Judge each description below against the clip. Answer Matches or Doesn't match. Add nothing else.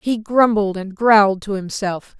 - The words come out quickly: Doesn't match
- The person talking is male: Doesn't match